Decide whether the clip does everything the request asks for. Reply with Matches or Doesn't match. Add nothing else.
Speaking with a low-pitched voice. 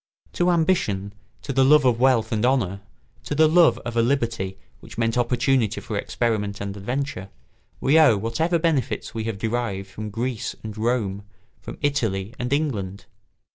Matches